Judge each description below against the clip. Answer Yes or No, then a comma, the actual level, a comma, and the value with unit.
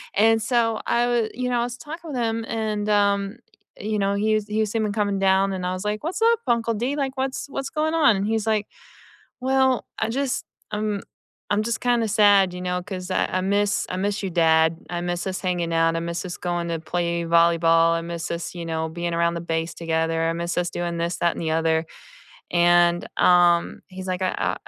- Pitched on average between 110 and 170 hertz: No, high, 190 Hz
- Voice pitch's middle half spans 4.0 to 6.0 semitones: Yes, average, 4.5 semitones